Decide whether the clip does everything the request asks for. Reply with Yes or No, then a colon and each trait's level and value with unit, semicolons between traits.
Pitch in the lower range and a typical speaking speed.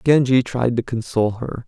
Yes: low, 120 Hz; average, 180 wpm